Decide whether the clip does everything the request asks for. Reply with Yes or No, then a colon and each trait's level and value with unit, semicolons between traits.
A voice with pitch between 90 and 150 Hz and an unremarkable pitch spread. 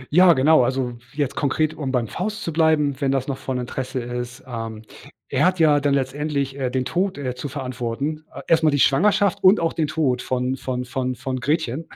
Yes: low, 135 Hz; average, 3.6 semitones